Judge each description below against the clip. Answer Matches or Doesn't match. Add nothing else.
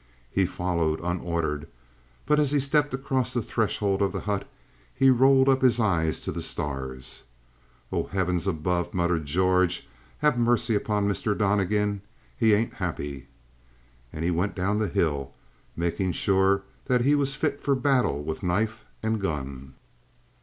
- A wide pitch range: Matches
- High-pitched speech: Doesn't match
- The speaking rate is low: Doesn't match